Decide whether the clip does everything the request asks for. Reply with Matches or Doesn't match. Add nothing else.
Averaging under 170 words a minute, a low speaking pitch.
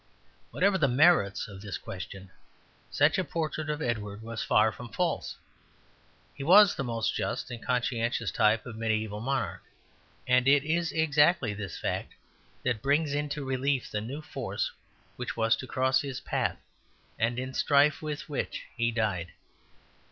Matches